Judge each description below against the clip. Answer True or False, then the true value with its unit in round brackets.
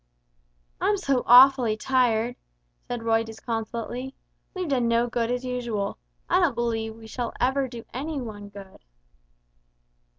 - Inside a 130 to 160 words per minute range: True (140 wpm)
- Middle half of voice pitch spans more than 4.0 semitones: False (2.6 semitones)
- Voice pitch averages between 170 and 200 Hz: False (240 Hz)